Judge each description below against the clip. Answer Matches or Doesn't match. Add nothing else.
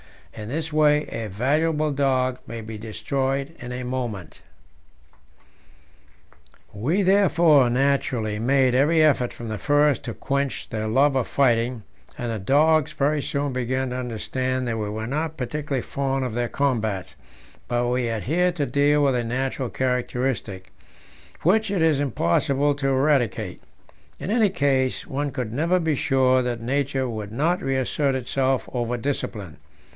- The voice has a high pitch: Doesn't match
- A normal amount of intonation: Matches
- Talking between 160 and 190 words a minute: Doesn't match